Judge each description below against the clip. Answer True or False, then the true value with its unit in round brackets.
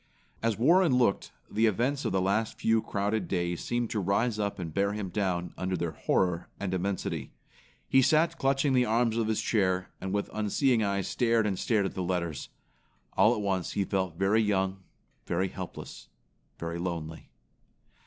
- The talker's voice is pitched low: True (100 Hz)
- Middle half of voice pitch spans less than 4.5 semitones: True (3.5 semitones)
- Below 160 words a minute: False (175 wpm)